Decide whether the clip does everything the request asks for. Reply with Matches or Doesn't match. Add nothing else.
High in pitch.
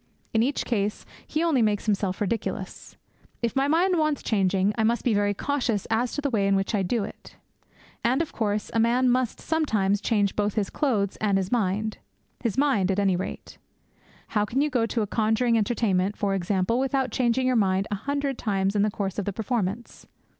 Matches